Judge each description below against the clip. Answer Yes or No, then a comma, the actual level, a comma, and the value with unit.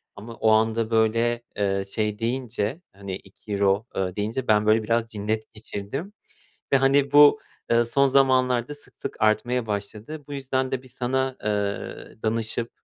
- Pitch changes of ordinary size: Yes, average, 3.6 semitones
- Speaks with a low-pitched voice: Yes, low, 115 Hz